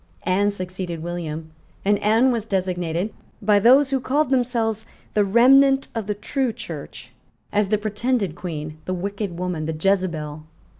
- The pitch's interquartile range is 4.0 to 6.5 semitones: Yes, average, 4.7 semitones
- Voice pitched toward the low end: No, high, 200 Hz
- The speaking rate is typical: Yes, average, 150 wpm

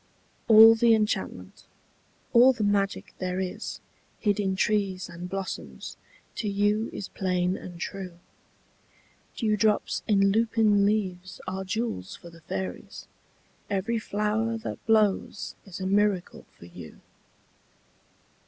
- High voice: Yes, high, 200 Hz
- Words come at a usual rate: No, slow, 120 wpm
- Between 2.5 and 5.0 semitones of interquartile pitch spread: Yes, average, 2.8 semitones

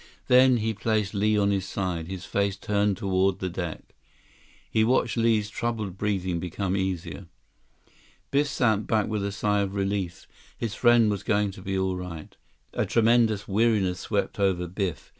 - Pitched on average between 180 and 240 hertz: No, low, 100 Hz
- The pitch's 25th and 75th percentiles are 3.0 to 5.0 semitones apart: No, narrow, 2.6 semitones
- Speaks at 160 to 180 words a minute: Yes, average, 165 wpm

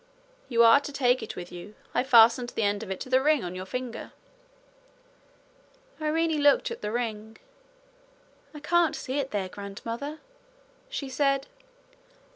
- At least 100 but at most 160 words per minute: Yes, average, 155 wpm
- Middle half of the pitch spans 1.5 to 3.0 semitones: No, average, 5.1 semitones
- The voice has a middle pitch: No, high, 245 Hz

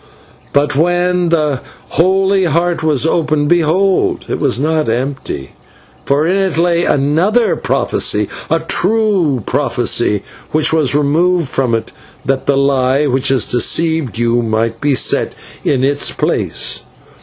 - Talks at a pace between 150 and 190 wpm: No, slow, 135 wpm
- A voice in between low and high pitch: Yes, medium, 150 Hz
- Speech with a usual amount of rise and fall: Yes, average, 4.5 semitones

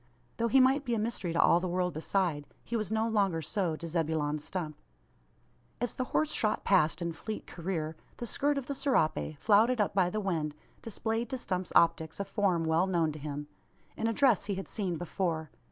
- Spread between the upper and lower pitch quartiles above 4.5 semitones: Yes, wide, 5.5 semitones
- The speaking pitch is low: No, medium, 185 Hz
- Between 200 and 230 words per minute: Yes, fast, 205 wpm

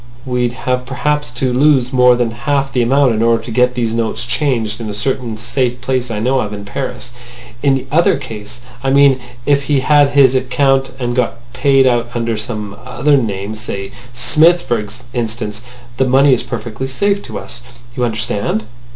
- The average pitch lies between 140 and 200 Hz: No, low, 125 Hz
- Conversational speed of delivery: Yes, average, 180 wpm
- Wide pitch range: No, narrow, 2.5 semitones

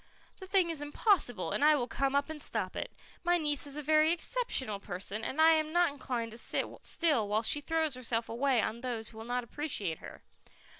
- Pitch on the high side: Yes, very high, 280 Hz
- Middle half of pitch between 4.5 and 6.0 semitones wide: Yes, wide, 5.5 semitones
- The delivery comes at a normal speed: No, fast, 215 wpm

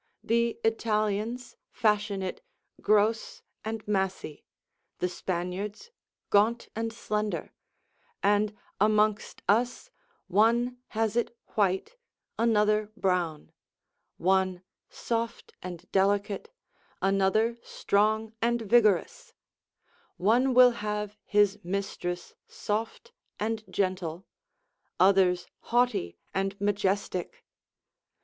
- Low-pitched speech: No, high, 210 Hz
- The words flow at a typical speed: No, slow, 85 wpm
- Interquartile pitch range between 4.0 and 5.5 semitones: No, average, 2.7 semitones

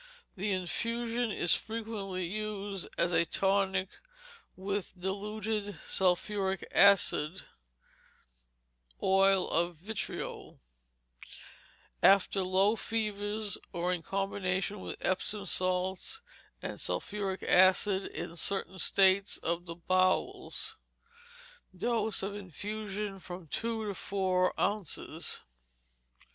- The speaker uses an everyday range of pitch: No, narrow, 2.1 semitones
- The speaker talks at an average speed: No, slow, 95 wpm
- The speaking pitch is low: No, high, 195 Hz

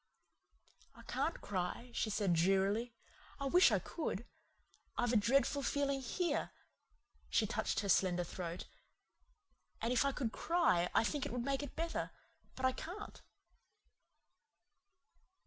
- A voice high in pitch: Yes, high, 240 Hz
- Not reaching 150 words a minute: Yes, average, 140 wpm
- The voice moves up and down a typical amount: No, wide, 6.2 semitones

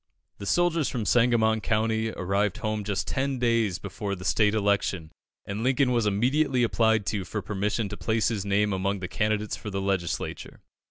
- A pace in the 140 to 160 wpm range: No, average, 175 wpm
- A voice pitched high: No, low, 105 Hz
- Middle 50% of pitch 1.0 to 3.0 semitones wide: Yes, narrow, 2.6 semitones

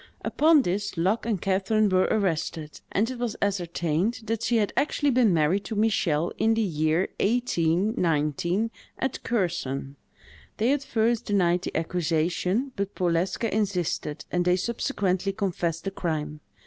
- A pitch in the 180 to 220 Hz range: Yes, high, 190 Hz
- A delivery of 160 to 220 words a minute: No, average, 145 wpm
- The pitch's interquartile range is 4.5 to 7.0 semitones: Yes, average, 4.8 semitones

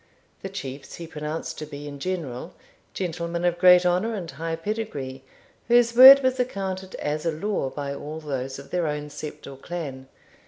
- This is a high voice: No, medium, 165 Hz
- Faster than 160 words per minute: Yes, average, 180 wpm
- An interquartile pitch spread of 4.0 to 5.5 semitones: Yes, average, 4.6 semitones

